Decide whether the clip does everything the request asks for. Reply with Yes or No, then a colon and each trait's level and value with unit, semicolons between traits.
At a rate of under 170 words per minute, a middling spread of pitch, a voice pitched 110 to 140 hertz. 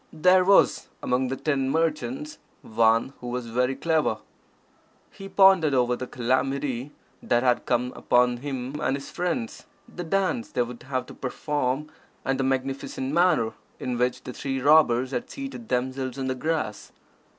Yes: average, 160 wpm; average, 3.8 semitones; low, 135 Hz